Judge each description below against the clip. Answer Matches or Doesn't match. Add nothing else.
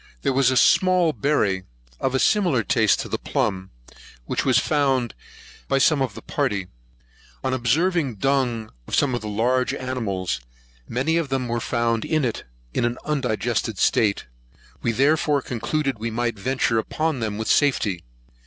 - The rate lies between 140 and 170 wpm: Matches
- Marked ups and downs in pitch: Doesn't match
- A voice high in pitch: Doesn't match